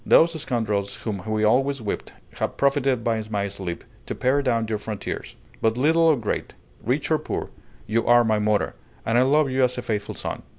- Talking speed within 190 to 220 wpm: Yes, average, 200 wpm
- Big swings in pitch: No, average, 4.0 semitones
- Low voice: Yes, low, 120 Hz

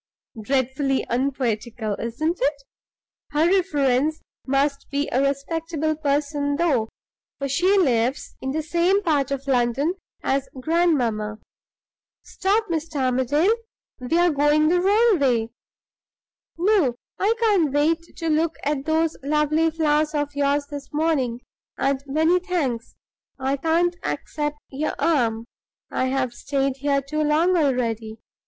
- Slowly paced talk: Yes, slow, 130 wpm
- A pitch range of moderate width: Yes, average, 3.6 semitones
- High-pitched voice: Yes, very high, 290 Hz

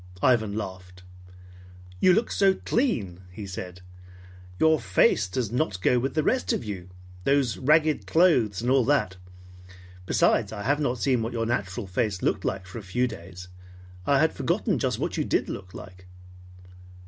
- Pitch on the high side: No, low, 115 Hz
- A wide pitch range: Yes, wide, 6.6 semitones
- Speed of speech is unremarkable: Yes, average, 170 wpm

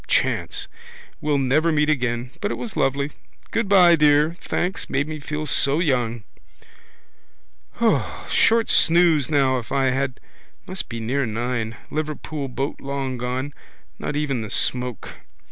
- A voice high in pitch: No, medium, 140 Hz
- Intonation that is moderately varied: Yes, average, 3.4 semitones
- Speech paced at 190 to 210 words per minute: No, slow, 135 wpm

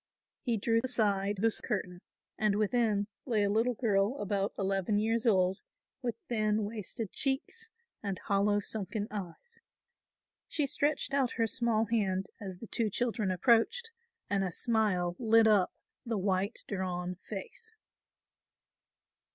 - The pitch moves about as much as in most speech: Yes, average, 3.0 semitones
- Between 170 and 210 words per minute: No, slow, 135 wpm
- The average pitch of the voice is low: No, high, 215 Hz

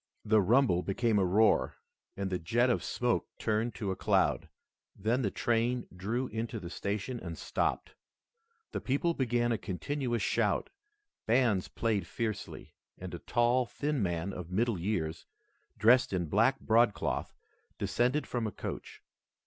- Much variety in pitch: No, average, 4.1 semitones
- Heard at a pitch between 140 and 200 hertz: No, low, 110 Hz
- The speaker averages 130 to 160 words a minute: Yes, average, 150 wpm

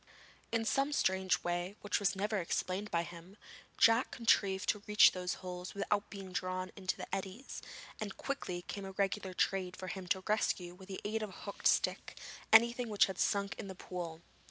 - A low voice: No, high, 195 Hz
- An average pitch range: No, narrow, 2.2 semitones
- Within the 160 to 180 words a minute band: No, average, 195 wpm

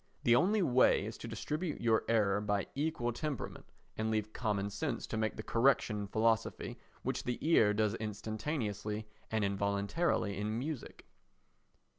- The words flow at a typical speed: Yes, average, 150 wpm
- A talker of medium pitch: No, low, 110 Hz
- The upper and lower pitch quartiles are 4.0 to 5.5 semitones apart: No, average, 3.3 semitones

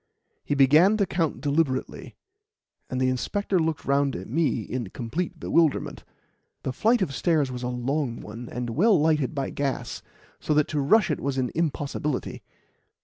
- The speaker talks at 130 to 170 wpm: Yes, average, 165 wpm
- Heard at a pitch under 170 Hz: Yes, medium, 140 Hz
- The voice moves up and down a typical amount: Yes, average, 4.1 semitones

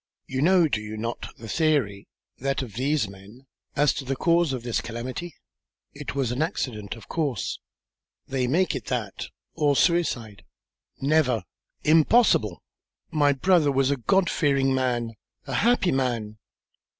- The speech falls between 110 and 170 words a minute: Yes, average, 150 wpm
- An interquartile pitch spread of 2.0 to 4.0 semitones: No, average, 5.0 semitones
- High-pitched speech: No, low, 135 Hz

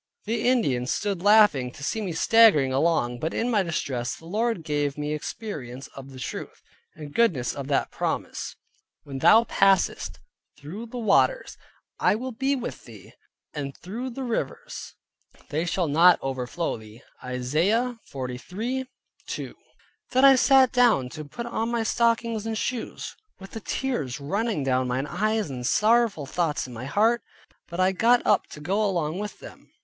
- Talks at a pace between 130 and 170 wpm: Yes, average, 165 wpm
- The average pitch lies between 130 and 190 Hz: Yes, medium, 185 Hz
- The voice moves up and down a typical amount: No, wide, 8.5 semitones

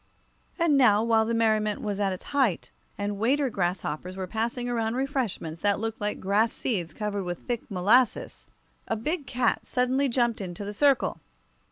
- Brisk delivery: No, average, 170 wpm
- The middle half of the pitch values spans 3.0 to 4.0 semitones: Yes, average, 3.7 semitones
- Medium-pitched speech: No, high, 220 Hz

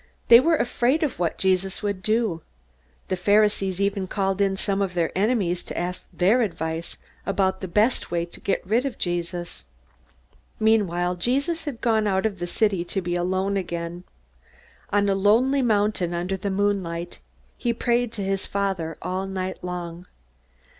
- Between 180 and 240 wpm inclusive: No, average, 165 wpm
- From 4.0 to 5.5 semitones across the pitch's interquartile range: No, average, 3.3 semitones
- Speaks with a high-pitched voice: Yes, high, 195 Hz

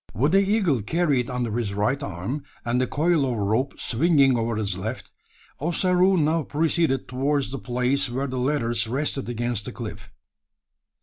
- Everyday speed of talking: Yes, average, 165 wpm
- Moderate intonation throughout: Yes, average, 4.3 semitones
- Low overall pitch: Yes, low, 130 Hz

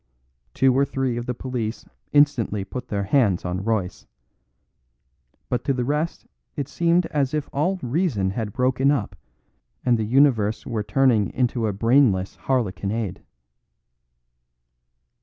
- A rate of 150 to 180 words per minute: No, slow, 135 wpm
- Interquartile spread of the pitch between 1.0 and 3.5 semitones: No, average, 4.5 semitones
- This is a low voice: Yes, low, 125 Hz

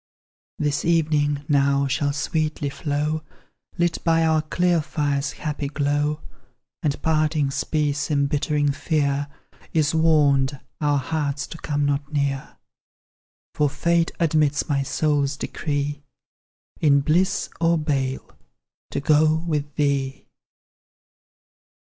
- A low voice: No, medium, 150 Hz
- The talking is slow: Yes, slow, 110 wpm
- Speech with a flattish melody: Yes, narrow, 1.7 semitones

